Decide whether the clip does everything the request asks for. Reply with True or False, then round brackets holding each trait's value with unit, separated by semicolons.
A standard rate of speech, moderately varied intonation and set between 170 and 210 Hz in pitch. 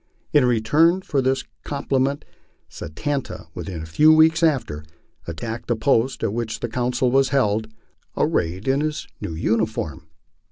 False (150 wpm; 4.5 semitones; 125 Hz)